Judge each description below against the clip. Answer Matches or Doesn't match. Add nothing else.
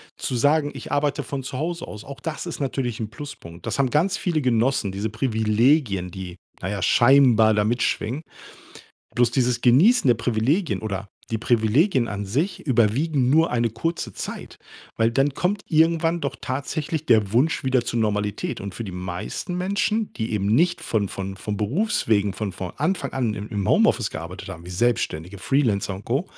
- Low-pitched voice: Matches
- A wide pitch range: Matches